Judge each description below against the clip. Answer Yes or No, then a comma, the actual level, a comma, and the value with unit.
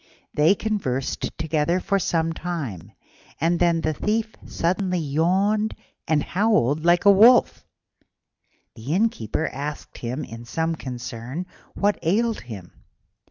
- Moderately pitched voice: Yes, medium, 165 Hz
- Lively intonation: Yes, wide, 6.1 semitones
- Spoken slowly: Yes, slow, 120 wpm